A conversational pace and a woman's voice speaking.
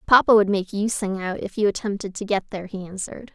No: fast, 250 wpm; female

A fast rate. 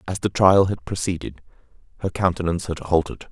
No: average, 165 wpm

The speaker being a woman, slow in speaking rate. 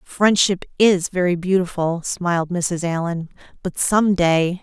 Yes: female; slow, 130 wpm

